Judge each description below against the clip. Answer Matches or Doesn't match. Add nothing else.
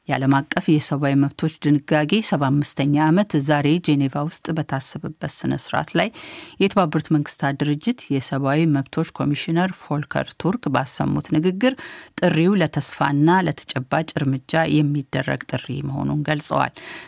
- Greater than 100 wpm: Matches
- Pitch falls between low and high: Matches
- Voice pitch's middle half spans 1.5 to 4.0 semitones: Matches